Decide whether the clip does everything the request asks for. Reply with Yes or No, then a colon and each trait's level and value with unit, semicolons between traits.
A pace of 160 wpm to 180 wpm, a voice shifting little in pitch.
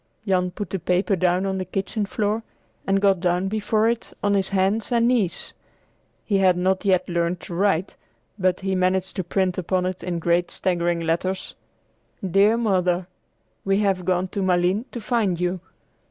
Yes: average, 175 wpm; narrow, 1.8 semitones